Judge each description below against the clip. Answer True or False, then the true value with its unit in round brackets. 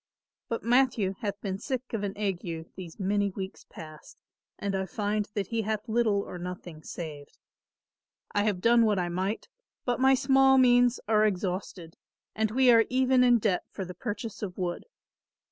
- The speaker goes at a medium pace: True (175 wpm)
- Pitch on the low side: False (205 Hz)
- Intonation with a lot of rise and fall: False (4.1 semitones)